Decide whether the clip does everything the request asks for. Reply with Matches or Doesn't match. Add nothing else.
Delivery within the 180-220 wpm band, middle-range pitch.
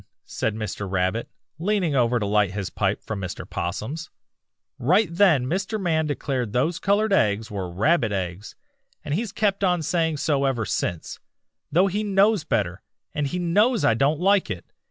Matches